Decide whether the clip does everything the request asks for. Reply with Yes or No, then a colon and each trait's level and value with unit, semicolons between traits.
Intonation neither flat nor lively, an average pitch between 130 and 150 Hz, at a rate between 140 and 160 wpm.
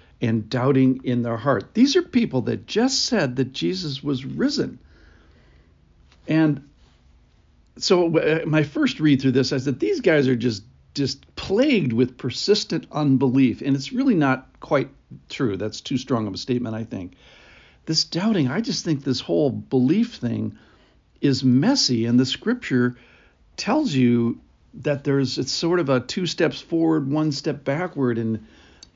Yes: average, 4.8 semitones; low, 135 Hz; average, 155 wpm